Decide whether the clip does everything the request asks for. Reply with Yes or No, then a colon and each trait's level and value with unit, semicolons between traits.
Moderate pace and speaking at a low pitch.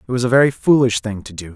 No: fast, 310 wpm; low, 120 Hz